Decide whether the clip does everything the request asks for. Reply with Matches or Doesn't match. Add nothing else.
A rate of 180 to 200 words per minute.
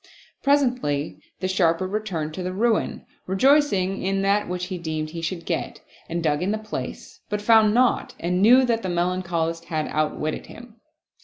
Doesn't match